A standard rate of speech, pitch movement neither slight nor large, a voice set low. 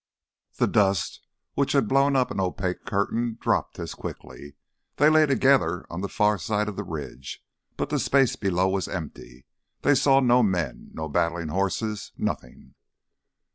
No: average, 155 wpm; wide, 5.8 semitones; low, 100 Hz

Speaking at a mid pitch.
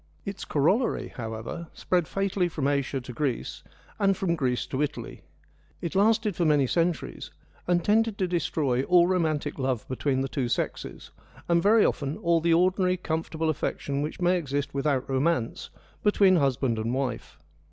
Yes: medium, 160 Hz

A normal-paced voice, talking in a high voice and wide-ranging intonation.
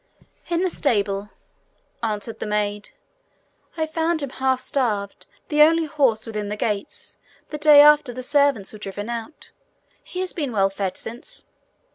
Yes: average, 155 wpm; high, 245 Hz; wide, 6.4 semitones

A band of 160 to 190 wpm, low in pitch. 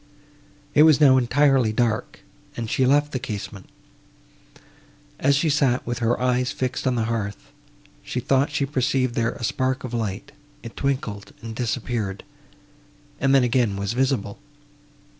No: average, 150 wpm; low, 125 Hz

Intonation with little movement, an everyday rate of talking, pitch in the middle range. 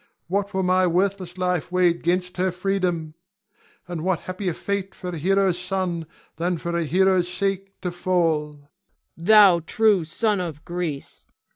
Yes: narrow, 2.0 semitones; average, 155 wpm; medium, 180 Hz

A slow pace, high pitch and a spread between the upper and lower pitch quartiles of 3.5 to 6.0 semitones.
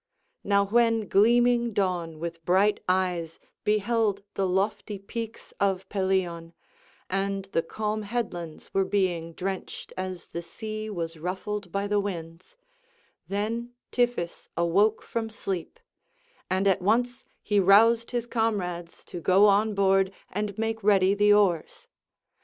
No: slow, 130 wpm; high, 200 Hz; average, 2.9 semitones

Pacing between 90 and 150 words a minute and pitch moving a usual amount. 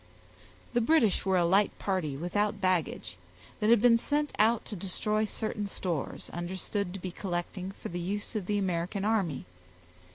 No: average, 165 wpm; average, 3.2 semitones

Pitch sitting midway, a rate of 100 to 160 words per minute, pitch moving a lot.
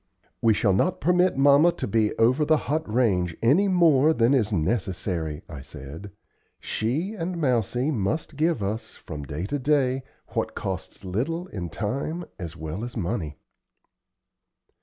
No: low, 115 Hz; average, 150 wpm; wide, 8.3 semitones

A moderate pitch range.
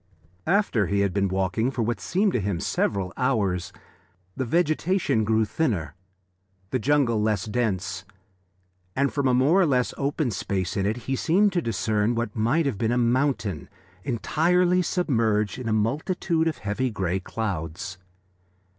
No: wide, 6.2 semitones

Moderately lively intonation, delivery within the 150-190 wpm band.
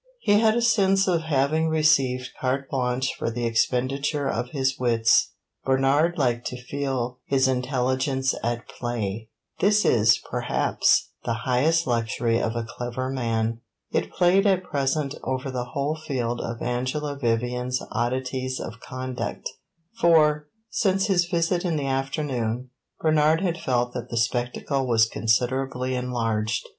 No: average, 3.7 semitones; average, 140 wpm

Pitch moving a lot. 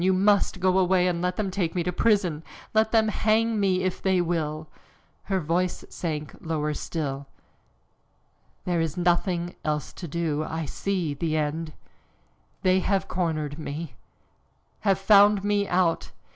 No: average, 3.2 semitones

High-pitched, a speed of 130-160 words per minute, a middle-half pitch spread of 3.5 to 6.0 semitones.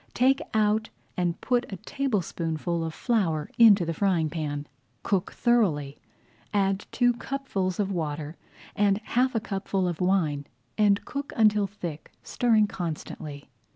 Yes: high, 195 Hz; slow, 135 wpm; average, 5.1 semitones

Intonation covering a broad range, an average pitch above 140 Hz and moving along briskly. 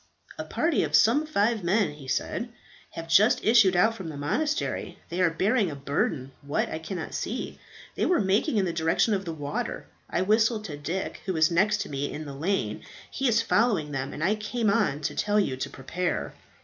Yes: wide, 6.2 semitones; medium, 185 Hz; fast, 210 wpm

